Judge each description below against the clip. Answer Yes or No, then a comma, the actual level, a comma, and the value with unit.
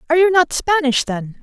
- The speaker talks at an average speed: No, fast, 210 wpm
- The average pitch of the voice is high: Yes, very high, 305 Hz